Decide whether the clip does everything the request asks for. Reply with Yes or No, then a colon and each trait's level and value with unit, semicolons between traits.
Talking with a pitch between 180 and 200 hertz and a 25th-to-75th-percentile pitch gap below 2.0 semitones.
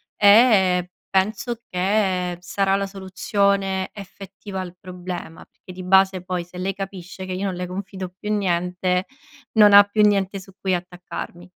Yes: high, 190 Hz; narrow, 1.6 semitones